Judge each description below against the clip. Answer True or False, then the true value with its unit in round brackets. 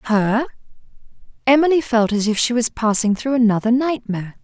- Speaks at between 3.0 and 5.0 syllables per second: False (5.4 syllables/s)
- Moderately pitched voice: False (230 Hz)